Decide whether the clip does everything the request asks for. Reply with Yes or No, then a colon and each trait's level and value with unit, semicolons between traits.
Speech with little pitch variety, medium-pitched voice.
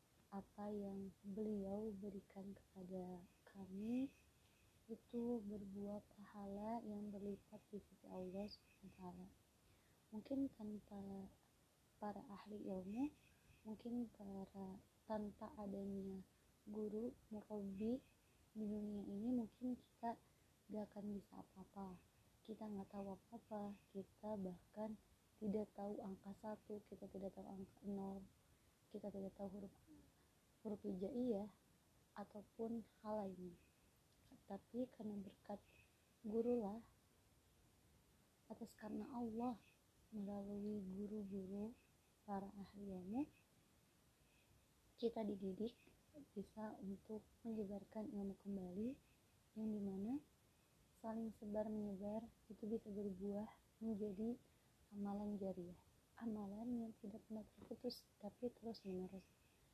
No: narrow, 1.9 semitones; high, 205 Hz